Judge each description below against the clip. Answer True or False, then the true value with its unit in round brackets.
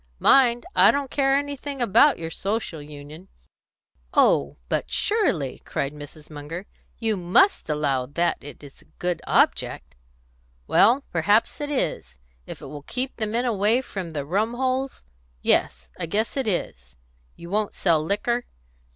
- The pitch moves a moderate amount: False (8.4 semitones)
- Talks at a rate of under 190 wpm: True (150 wpm)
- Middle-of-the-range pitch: False (195 Hz)